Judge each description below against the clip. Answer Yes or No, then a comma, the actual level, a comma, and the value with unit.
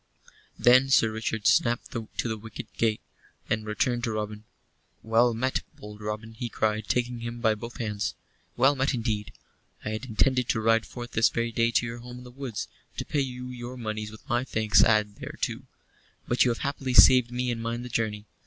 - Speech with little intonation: Yes, narrow, 2.2 semitones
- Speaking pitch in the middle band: No, low, 115 Hz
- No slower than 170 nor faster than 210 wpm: Yes, average, 200 wpm